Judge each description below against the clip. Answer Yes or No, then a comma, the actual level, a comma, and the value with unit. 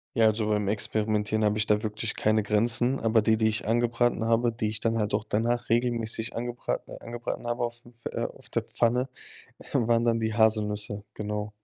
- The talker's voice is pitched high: No, low, 110 Hz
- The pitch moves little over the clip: Yes, narrow, 1.8 semitones